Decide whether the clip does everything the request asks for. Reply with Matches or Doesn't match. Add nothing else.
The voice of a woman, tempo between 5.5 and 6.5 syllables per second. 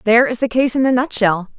Matches